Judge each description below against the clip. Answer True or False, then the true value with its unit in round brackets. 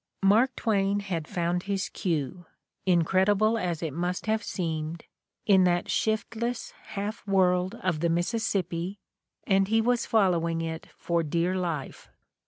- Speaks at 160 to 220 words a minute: False (140 wpm)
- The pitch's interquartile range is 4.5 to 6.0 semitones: False (3.4 semitones)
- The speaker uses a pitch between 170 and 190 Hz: True (185 Hz)